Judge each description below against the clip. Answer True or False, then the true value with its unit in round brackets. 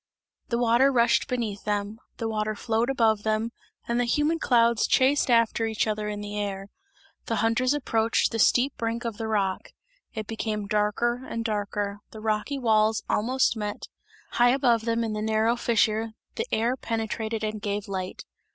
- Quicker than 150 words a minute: True (170 wpm)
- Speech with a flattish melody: True (2.0 semitones)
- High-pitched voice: True (225 Hz)